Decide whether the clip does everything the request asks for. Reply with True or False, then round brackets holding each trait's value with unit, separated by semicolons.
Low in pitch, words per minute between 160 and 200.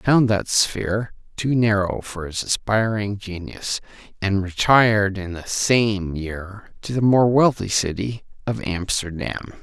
False (105 Hz; 145 wpm)